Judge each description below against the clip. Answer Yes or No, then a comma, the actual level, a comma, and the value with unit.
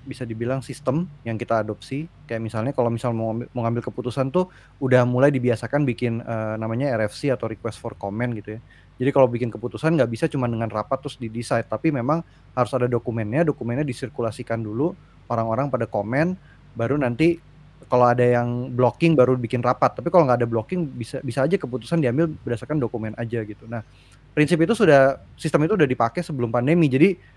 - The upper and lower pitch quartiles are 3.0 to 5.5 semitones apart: Yes, average, 3.7 semitones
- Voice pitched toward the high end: No, low, 125 Hz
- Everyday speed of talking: No, fast, 180 wpm